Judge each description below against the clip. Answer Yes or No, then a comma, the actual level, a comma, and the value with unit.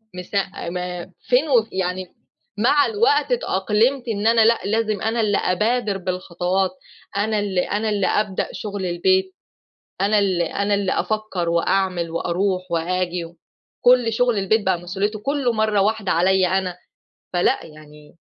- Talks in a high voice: Yes, high, 200 Hz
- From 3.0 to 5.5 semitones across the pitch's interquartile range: Yes, average, 3.4 semitones